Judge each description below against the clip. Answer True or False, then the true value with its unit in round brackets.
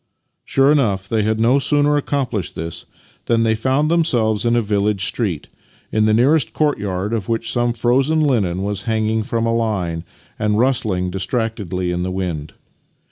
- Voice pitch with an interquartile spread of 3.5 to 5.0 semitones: True (4.4 semitones)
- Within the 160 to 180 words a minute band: True (165 wpm)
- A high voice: False (110 Hz)